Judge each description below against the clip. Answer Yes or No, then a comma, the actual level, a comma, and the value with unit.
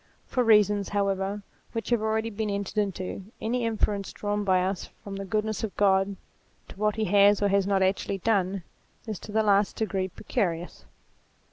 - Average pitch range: No, narrow, 1.9 semitones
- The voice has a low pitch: No, high, 200 Hz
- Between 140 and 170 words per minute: No, average, 180 wpm